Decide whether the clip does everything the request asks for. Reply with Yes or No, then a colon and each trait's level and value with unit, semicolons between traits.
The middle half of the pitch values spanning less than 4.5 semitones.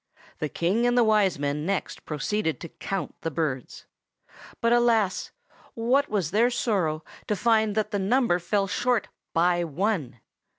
No: average, 5.3 semitones